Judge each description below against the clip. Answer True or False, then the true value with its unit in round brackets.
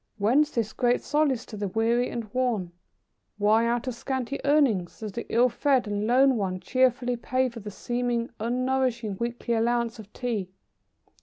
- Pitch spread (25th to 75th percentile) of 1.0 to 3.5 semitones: True (2.7 semitones)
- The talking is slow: False (165 wpm)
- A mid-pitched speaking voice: False (235 Hz)